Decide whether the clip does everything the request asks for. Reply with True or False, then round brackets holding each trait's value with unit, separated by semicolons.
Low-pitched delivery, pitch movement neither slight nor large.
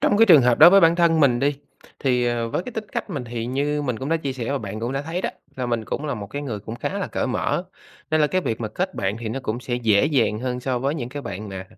True (130 Hz; 4.3 semitones)